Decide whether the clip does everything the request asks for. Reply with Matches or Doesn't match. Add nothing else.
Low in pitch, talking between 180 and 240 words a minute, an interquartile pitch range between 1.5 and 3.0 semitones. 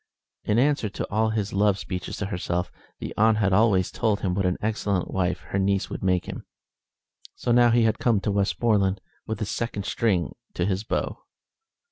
Matches